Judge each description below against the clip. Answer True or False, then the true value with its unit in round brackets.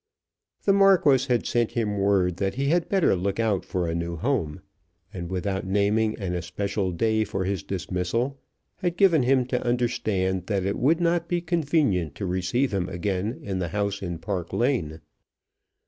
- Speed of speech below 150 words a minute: False (175 wpm)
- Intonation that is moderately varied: False (5.8 semitones)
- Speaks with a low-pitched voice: True (100 Hz)